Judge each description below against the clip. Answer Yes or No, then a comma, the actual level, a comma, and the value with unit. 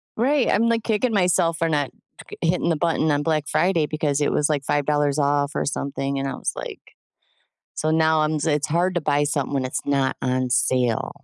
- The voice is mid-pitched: Yes, medium, 150 Hz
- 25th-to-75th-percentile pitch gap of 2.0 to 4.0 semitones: Yes, average, 2.8 semitones